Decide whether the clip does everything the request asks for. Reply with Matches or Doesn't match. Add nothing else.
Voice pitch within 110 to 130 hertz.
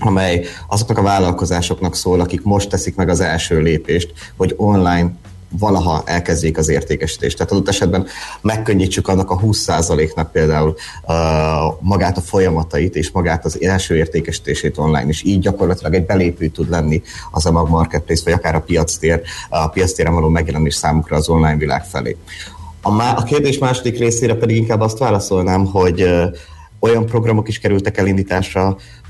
Doesn't match